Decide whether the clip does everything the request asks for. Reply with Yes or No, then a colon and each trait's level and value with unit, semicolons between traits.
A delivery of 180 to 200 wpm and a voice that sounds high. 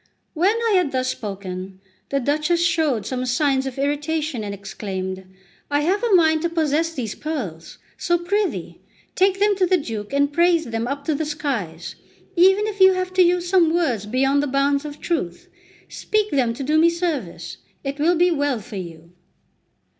Yes: average, 185 wpm; very high, 290 Hz